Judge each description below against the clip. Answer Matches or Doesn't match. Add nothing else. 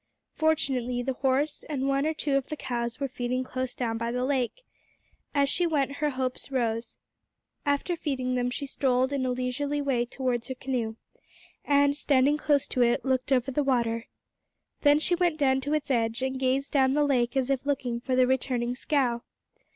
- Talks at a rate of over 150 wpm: Matches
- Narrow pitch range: Matches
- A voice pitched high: Matches